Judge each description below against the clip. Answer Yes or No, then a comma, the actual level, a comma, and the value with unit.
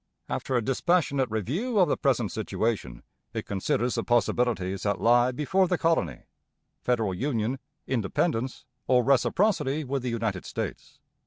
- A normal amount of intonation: Yes, average, 4.3 semitones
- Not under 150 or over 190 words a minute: No, average, 140 wpm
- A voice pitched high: No, low, 125 Hz